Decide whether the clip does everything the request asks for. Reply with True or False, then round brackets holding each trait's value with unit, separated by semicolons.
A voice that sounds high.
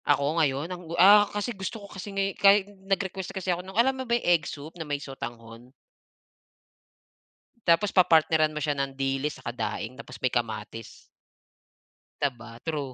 False (155 Hz)